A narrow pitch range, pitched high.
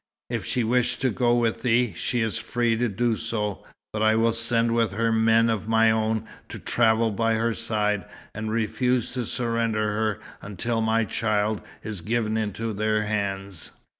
No: narrow, 1.3 semitones; low, 110 Hz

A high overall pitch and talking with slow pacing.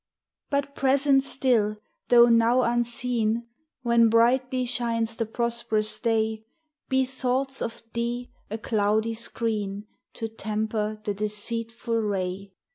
Yes: high, 230 Hz; slow, 115 wpm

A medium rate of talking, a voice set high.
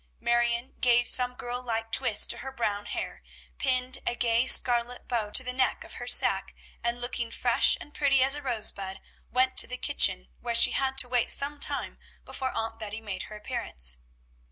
Yes: average, 190 wpm; high, 240 Hz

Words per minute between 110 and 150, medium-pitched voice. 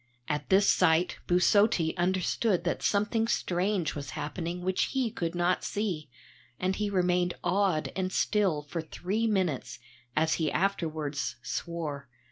Yes: slow, 135 wpm; medium, 180 Hz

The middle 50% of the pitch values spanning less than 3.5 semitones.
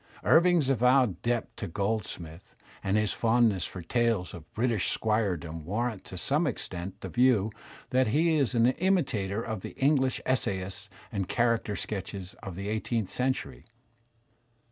No: average, 4.8 semitones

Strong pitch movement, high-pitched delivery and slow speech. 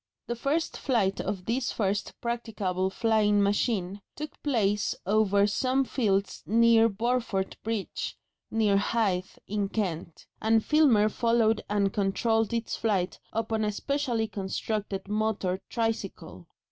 No: average, 2.7 semitones; high, 215 Hz; slow, 120 wpm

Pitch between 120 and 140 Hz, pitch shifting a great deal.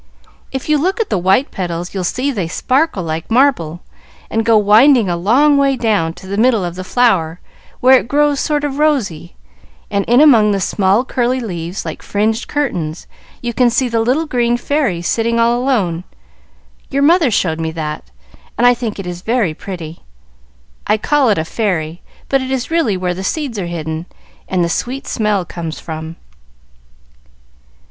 No: high, 220 Hz; wide, 6.7 semitones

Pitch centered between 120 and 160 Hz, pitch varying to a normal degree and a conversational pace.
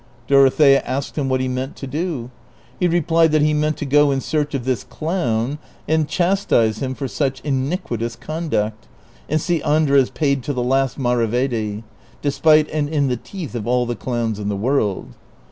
Yes: low, 135 Hz; average, 3.9 semitones; average, 180 wpm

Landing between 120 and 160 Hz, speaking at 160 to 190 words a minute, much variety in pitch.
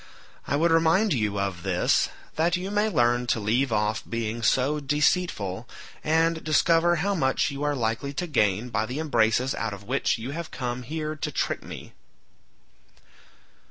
Yes: low, 135 Hz; average, 165 wpm; wide, 6.1 semitones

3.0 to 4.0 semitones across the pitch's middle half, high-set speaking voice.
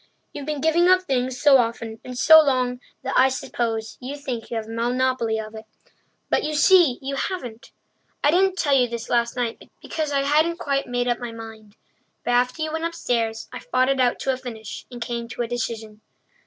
Yes: average, 3.6 semitones; very high, 250 Hz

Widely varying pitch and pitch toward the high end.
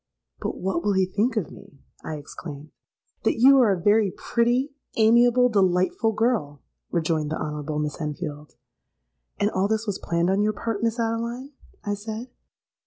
Yes: wide, 6.4 semitones; high, 200 Hz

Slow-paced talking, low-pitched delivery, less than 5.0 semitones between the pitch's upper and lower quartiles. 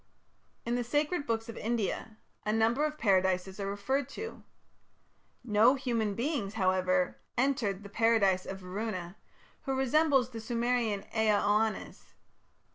No: slow, 130 wpm; high, 225 Hz; average, 3.9 semitones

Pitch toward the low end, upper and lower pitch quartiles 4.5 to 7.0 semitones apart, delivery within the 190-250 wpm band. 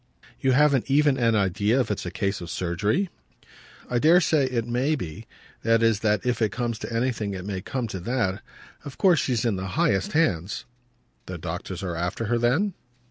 Yes: low, 115 Hz; average, 5.3 semitones; average, 195 wpm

